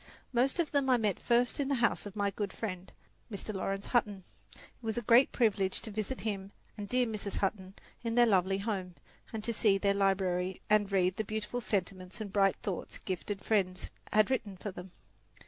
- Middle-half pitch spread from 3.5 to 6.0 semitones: No, average, 2.9 semitones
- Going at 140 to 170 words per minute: No, average, 195 wpm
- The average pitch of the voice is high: Yes, high, 205 Hz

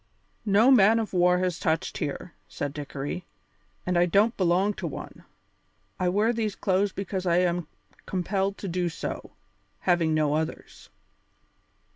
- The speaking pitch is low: No, medium, 180 Hz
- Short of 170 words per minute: Yes, average, 145 wpm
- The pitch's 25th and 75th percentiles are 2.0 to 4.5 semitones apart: Yes, average, 2.8 semitones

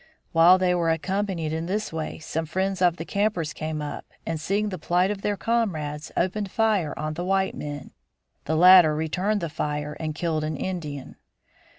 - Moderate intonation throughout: Yes, average, 3.7 semitones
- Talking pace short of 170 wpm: No, average, 185 wpm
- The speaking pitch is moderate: Yes, medium, 170 Hz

